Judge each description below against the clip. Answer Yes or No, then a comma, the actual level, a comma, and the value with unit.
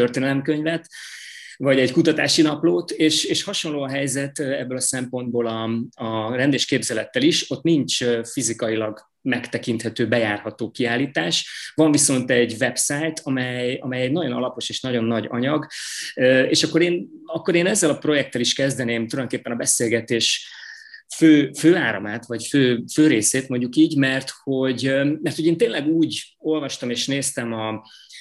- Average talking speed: Yes, average, 145 wpm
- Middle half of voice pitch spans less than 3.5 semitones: No, average, 4.5 semitones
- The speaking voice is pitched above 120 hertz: Yes, low, 130 Hz